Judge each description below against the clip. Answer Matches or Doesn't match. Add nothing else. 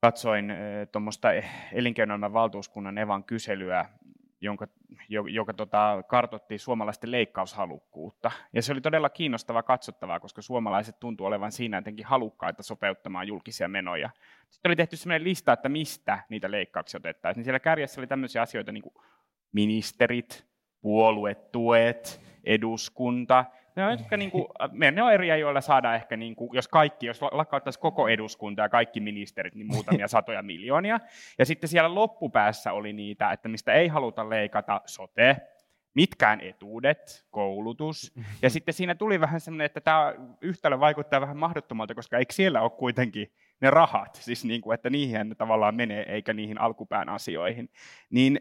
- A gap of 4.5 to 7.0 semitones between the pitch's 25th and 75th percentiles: Matches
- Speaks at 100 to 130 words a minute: Doesn't match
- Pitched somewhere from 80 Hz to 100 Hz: Doesn't match